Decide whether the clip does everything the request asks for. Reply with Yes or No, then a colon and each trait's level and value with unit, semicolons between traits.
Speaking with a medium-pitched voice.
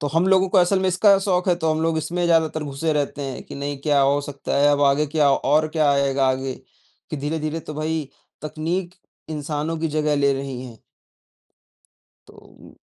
Yes: medium, 150 Hz